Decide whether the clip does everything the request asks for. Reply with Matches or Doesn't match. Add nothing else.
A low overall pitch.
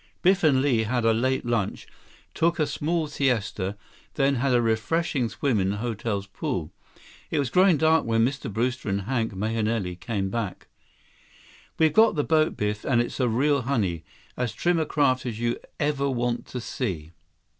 Matches